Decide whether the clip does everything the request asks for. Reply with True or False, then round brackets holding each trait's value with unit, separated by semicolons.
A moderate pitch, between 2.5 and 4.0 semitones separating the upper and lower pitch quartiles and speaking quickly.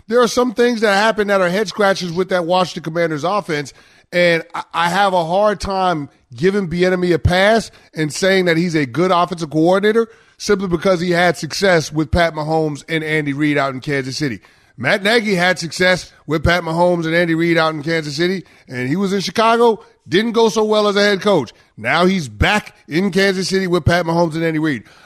True (175 Hz; 3.5 semitones; 210 wpm)